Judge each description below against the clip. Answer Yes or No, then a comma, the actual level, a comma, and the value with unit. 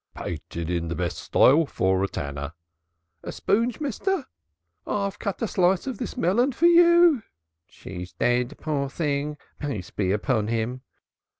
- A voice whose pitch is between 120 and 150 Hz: Yes, medium, 140 Hz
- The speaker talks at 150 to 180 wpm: Yes, average, 165 wpm